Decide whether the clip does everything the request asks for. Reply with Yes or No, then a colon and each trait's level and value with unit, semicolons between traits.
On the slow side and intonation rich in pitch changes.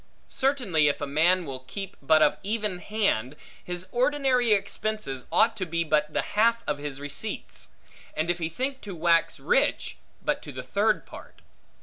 No: average, 180 wpm; wide, 6.3 semitones